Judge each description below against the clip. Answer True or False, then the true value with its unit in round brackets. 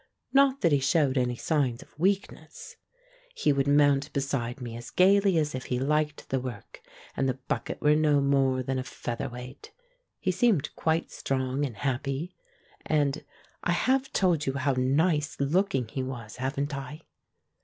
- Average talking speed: True (165 wpm)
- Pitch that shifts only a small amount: False (3.3 semitones)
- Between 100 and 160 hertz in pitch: True (140 Hz)